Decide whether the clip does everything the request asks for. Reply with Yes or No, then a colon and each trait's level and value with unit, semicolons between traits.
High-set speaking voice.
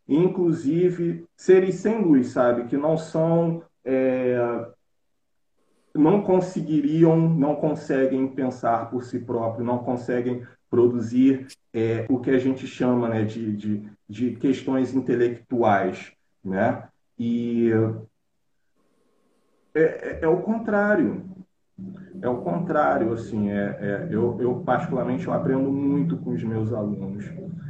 No: low, 130 Hz